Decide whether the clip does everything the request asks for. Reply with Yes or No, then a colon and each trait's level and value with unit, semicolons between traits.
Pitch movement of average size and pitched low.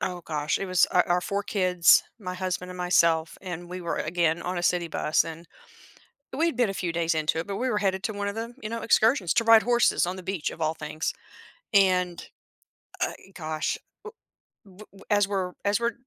No: average, 3.1 semitones; medium, 185 Hz